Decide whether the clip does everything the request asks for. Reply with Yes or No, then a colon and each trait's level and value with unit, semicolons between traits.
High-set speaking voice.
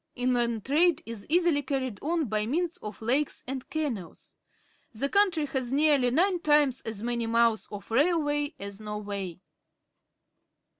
Yes: very high, 260 Hz